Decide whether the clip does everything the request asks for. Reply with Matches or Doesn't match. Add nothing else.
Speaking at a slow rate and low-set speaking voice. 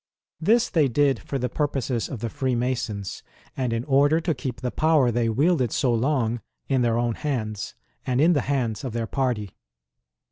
Doesn't match